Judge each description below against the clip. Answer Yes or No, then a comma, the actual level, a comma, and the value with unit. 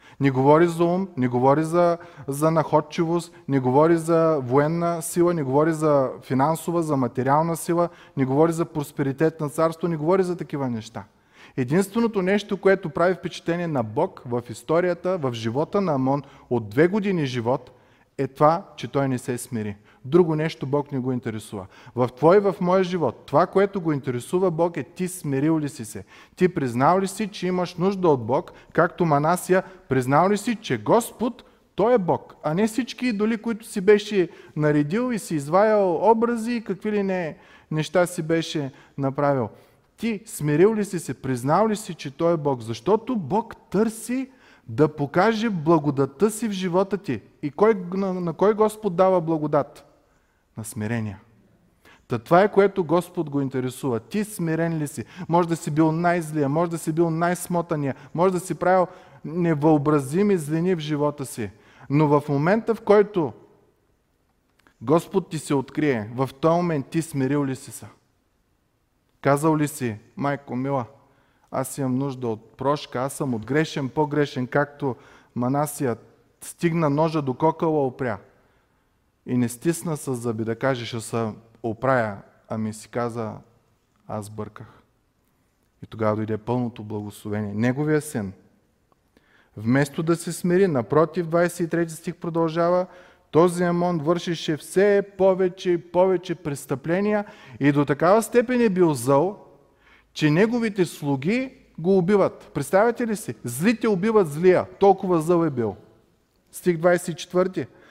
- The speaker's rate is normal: Yes, average, 155 wpm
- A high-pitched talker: No, medium, 155 Hz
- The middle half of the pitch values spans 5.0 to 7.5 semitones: Yes, wide, 5.5 semitones